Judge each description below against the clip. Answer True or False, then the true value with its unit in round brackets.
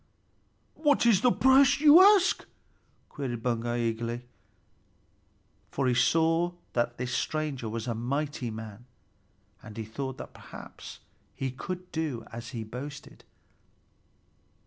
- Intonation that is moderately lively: False (5.9 semitones)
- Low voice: True (130 Hz)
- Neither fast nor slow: False (125 wpm)